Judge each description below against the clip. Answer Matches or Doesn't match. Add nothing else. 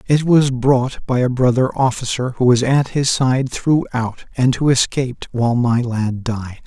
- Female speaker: Doesn't match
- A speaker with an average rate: Matches